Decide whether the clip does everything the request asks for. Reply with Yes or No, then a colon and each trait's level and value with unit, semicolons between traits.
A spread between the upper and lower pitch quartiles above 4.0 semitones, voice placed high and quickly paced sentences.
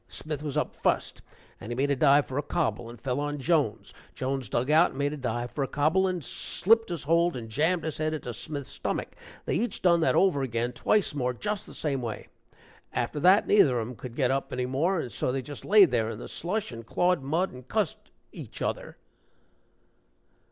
No: average, 5.1 semitones; medium, 145 Hz; fast, 220 wpm